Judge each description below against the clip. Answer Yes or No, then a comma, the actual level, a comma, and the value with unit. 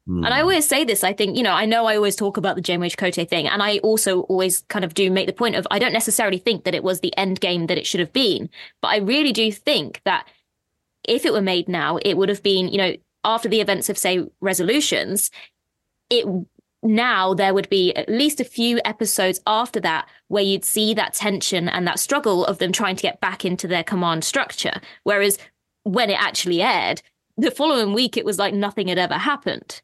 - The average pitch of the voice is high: Yes, high, 200 Hz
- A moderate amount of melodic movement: Yes, average, 3.2 semitones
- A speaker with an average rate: No, fast, 230 wpm